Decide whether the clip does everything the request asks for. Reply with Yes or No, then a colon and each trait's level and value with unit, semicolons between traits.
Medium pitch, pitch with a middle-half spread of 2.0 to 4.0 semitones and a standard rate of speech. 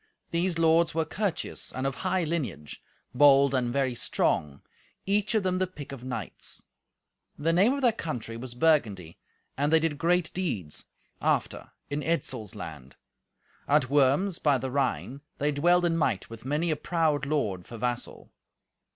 No: medium, 145 Hz; average, 5.2 semitones; average, 160 wpm